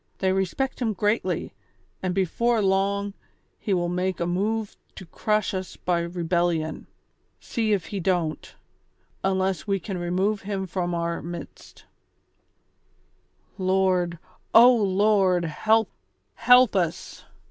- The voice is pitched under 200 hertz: Yes, high, 190 Hz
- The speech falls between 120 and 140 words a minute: Yes, slow, 135 wpm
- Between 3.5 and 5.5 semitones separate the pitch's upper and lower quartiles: No, average, 2.9 semitones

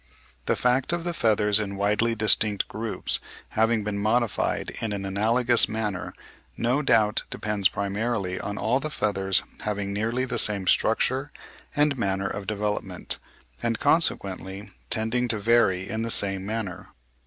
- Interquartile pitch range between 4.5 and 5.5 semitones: No, average, 2.7 semitones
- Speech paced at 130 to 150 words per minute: Yes, average, 145 wpm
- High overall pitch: No, low, 110 Hz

